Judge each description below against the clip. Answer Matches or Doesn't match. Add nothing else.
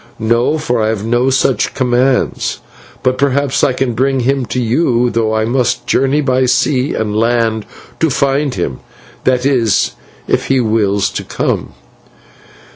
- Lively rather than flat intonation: Doesn't match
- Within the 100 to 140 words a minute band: Doesn't match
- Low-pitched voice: Matches